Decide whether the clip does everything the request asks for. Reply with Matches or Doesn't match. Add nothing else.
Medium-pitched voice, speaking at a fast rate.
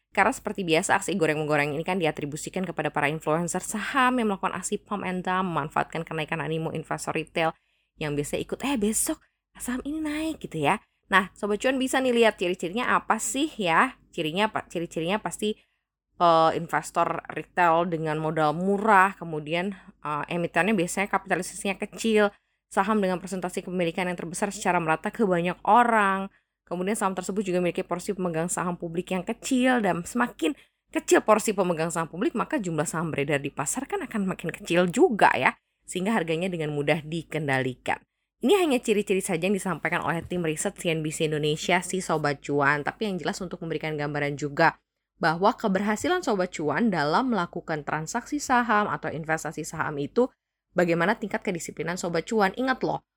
Matches